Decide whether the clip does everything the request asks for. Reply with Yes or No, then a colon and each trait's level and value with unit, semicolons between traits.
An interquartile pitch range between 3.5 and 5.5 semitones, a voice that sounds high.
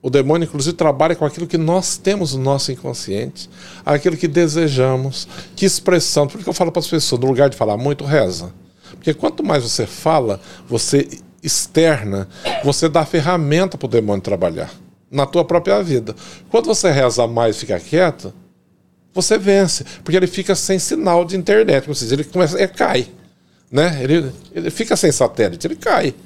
No: average, 4.8 semitones; medium, 155 Hz